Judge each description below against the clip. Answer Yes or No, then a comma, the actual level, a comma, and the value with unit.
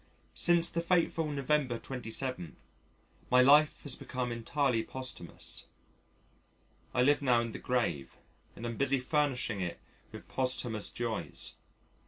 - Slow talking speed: Yes, slow, 125 wpm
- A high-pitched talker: No, low, 130 Hz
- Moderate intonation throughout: Yes, average, 3.6 semitones